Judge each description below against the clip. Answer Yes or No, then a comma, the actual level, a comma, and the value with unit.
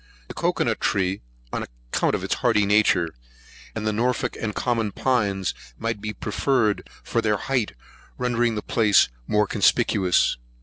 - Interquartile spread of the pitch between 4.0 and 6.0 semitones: No, average, 2.8 semitones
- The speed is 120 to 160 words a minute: Yes, average, 150 wpm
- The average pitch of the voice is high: No, low, 105 Hz